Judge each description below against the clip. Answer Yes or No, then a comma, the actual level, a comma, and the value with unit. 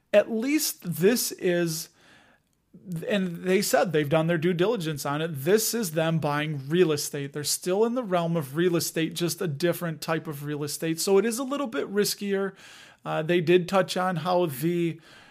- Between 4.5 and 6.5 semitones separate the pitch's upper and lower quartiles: No, average, 3.4 semitones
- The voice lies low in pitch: No, medium, 175 Hz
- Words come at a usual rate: Yes, average, 190 wpm